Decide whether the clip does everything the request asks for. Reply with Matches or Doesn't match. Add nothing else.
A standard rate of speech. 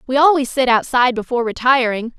Matches